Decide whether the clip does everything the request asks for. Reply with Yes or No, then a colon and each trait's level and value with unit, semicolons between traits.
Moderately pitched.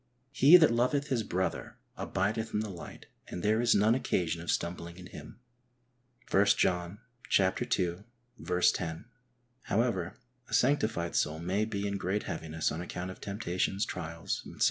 No: very low, 95 Hz